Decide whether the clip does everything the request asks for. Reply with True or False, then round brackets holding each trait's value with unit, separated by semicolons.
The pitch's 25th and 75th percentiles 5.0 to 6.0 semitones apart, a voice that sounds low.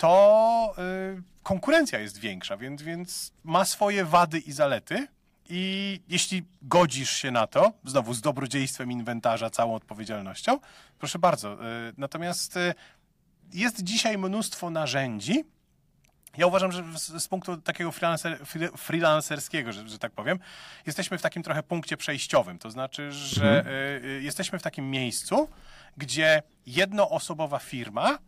False (5.3 semitones; 165 Hz)